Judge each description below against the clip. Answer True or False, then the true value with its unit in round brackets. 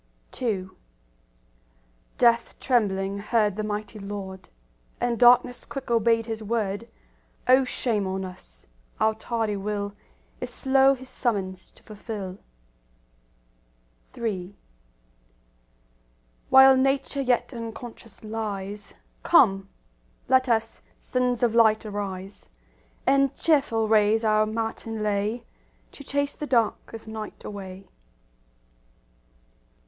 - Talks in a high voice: True (220 Hz)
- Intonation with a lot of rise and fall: False (3.1 semitones)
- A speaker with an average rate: False (105 wpm)